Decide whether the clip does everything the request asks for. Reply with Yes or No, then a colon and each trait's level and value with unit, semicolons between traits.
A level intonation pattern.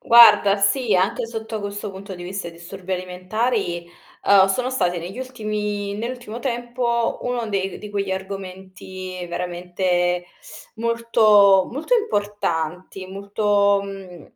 No: average, 3.4 semitones